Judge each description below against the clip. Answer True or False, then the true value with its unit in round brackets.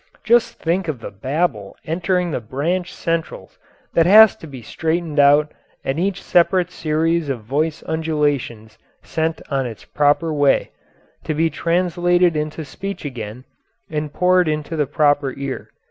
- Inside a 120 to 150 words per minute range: True (145 wpm)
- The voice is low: False (155 Hz)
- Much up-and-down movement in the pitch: False (3.5 semitones)